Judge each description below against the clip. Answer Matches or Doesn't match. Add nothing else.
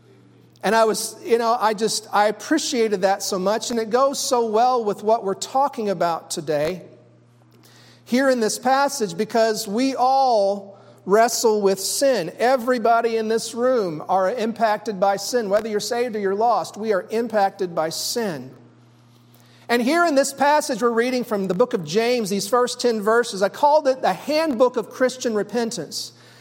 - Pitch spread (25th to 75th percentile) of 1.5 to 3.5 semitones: Doesn't match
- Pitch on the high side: Matches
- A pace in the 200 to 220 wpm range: Doesn't match